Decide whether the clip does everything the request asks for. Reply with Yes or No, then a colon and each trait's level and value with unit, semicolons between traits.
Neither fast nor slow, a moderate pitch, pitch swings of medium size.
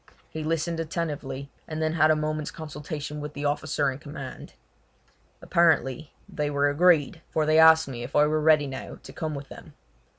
No: average, 185 wpm; medium, 150 Hz; narrow, 1.8 semitones